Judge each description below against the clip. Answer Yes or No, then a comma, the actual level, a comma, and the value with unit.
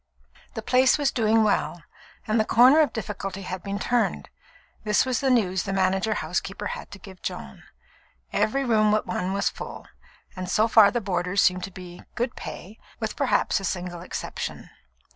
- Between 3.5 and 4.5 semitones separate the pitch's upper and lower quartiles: Yes, average, 3.8 semitones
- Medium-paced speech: Yes, average, 180 wpm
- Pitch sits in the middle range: No, high, 210 Hz